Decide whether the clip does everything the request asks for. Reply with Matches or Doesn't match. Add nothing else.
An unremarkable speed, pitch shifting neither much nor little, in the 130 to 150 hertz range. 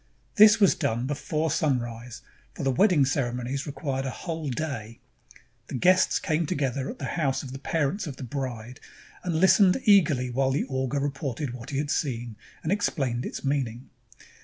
Matches